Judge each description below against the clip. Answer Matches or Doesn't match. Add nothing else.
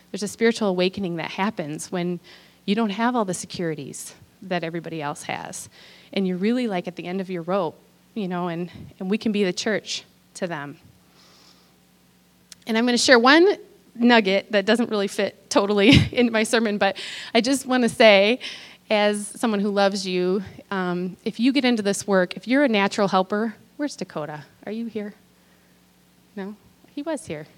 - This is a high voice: Matches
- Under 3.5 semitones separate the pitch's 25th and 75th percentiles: Doesn't match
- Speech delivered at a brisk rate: Doesn't match